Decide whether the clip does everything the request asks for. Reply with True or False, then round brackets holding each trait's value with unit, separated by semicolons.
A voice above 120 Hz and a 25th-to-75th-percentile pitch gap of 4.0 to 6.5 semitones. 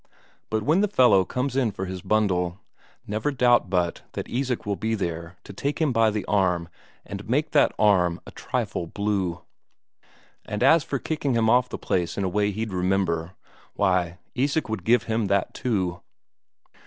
False (105 Hz; 4.9 semitones)